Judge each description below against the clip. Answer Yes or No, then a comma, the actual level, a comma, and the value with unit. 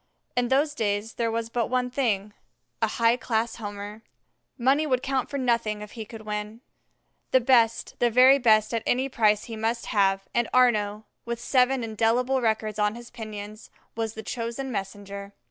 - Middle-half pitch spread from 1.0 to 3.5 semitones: Yes, average, 2.8 semitones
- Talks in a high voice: Yes, high, 230 Hz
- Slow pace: No, average, 175 wpm